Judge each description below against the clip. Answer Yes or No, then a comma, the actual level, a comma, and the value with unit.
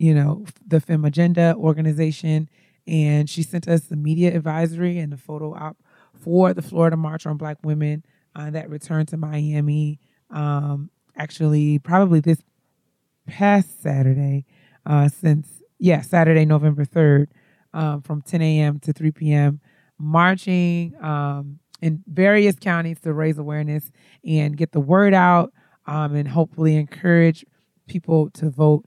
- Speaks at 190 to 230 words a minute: No, average, 140 wpm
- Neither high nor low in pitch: Yes, medium, 155 Hz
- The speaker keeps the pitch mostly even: Yes, narrow, 2.1 semitones